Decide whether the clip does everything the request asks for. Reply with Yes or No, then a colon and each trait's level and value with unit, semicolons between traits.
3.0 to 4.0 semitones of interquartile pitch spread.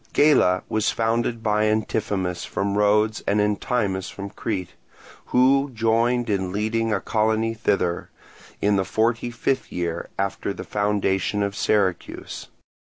No: narrow, 2.4 semitones